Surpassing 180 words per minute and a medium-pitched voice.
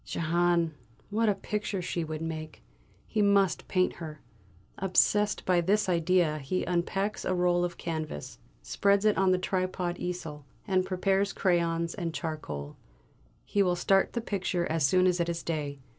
No: average, 160 wpm; medium, 180 Hz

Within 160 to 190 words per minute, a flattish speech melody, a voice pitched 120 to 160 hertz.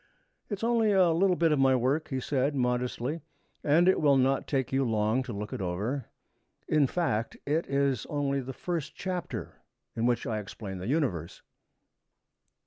No: average, 175 wpm; average, 4.8 semitones; low, 135 Hz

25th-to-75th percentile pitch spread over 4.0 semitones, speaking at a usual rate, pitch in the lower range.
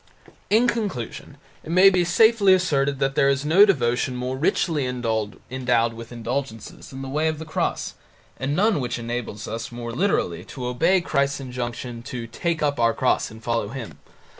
Yes: average, 5.1 semitones; average, 175 wpm; low, 130 Hz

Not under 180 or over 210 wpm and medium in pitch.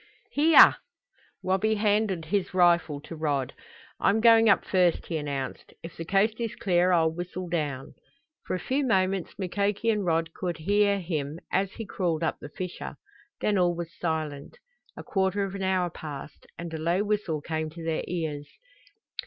No: average, 170 wpm; medium, 180 Hz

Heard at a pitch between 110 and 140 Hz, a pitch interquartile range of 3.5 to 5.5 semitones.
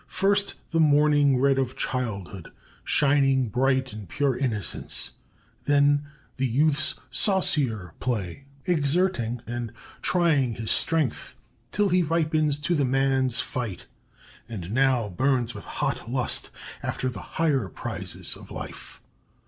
Yes: low, 135 Hz; average, 3.8 semitones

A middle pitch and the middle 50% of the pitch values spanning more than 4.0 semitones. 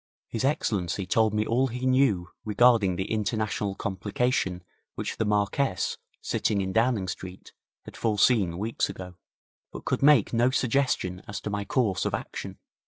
No: low, 105 Hz; average, 4.4 semitones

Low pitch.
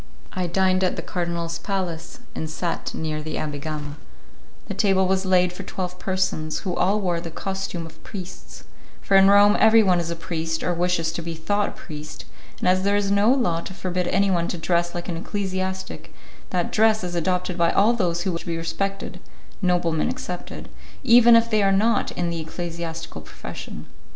No: medium, 180 Hz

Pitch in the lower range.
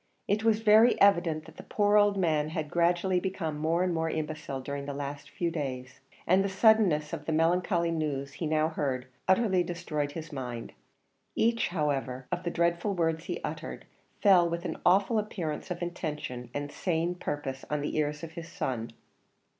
No: medium, 165 Hz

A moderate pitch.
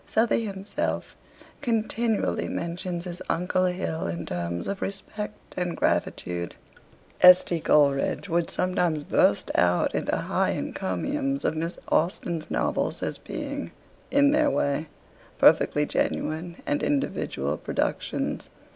Yes: medium, 180 Hz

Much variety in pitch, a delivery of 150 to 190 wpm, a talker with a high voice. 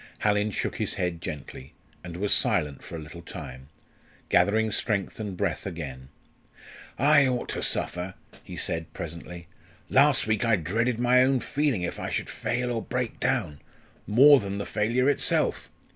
No: wide, 6.4 semitones; average, 160 wpm; low, 105 Hz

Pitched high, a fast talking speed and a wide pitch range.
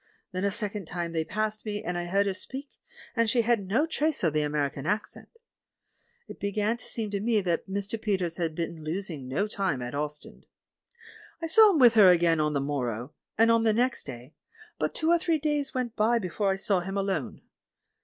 Yes: high, 195 Hz; fast, 210 wpm; wide, 5.7 semitones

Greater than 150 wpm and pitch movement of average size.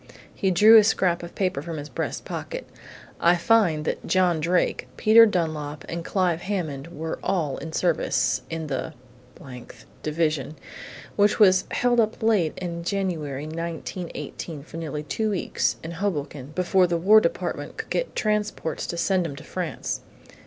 Yes: average, 160 wpm; average, 3.9 semitones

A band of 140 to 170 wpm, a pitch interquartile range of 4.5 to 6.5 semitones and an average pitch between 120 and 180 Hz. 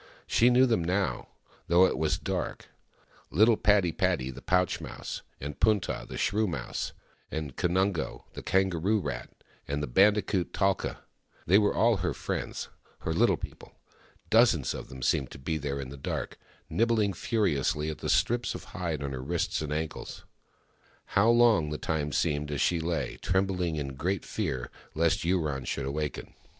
No: average, 165 wpm; average, 5.2 semitones; very low, 85 Hz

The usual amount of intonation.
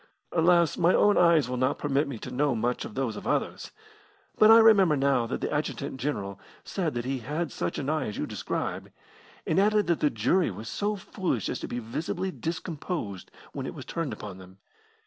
No: wide, 6.1 semitones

